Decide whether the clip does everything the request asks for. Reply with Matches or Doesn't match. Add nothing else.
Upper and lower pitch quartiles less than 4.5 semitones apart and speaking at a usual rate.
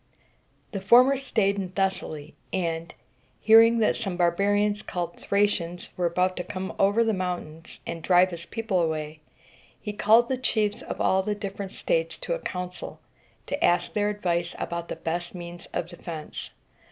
Matches